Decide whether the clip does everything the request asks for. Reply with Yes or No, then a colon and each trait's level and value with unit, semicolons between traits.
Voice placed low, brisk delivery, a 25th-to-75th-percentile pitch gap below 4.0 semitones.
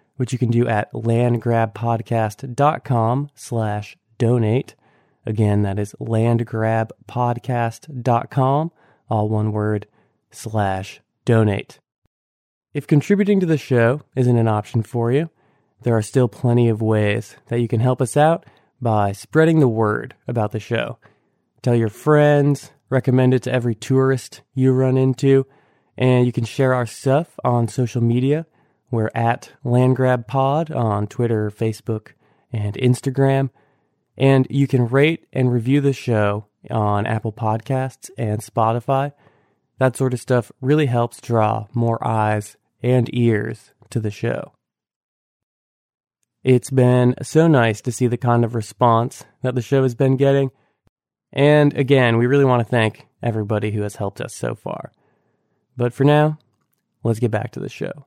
No: low, 120 Hz; average, 145 wpm; average, 3.2 semitones